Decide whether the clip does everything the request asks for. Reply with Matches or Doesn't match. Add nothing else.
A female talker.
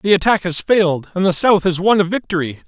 Doesn't match